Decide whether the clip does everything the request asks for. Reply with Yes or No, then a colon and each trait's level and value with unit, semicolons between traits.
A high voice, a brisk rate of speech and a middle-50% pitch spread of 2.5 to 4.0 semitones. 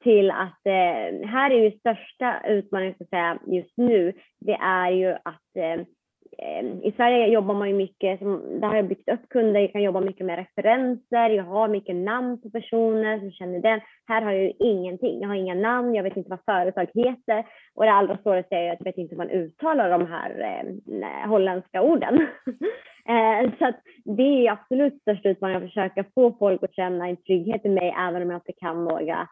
Yes: high, 200 Hz; fast, 205 wpm; average, 3.6 semitones